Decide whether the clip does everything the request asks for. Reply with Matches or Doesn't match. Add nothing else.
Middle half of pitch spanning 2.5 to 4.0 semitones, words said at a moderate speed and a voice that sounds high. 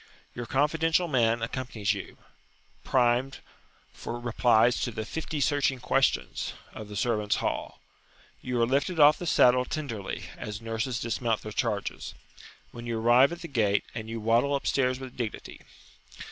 Doesn't match